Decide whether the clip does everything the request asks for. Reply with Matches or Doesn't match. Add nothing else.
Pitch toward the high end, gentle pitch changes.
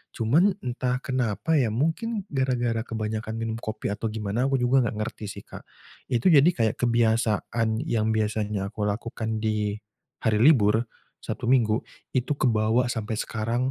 Doesn't match